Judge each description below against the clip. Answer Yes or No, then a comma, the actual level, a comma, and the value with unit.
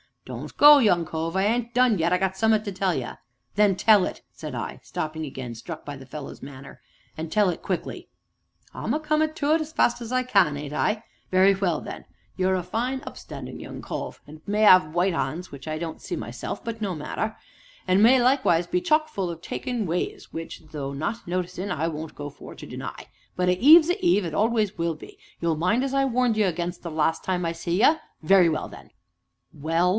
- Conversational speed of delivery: No, fast, 220 wpm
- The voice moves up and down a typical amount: No, wide, 5.7 semitones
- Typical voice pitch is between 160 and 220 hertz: Yes, medium, 185 Hz